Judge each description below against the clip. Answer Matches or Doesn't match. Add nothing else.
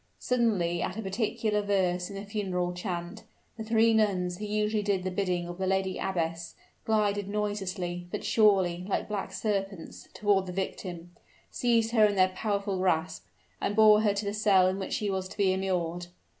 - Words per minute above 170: Matches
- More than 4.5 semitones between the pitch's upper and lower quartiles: Doesn't match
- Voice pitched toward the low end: Doesn't match